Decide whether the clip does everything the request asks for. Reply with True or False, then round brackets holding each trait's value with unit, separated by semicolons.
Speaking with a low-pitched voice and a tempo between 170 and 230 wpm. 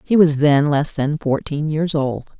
False (150 Hz; 200 wpm)